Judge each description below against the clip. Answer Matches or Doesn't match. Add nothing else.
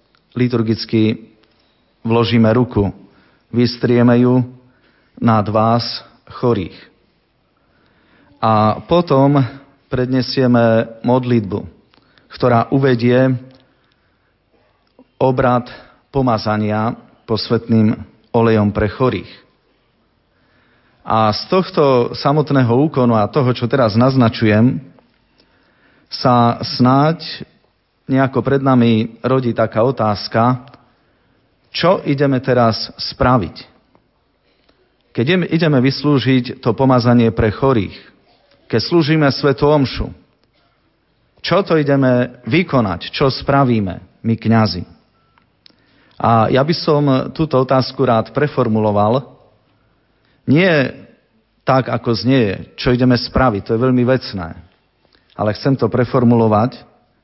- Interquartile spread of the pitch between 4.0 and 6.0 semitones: Doesn't match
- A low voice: Matches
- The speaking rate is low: Matches